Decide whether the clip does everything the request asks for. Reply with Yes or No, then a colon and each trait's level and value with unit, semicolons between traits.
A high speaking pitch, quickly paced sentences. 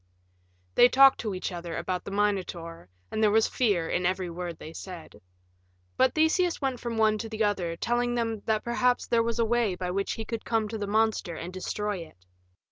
Yes: high, 215 Hz; fast, 210 wpm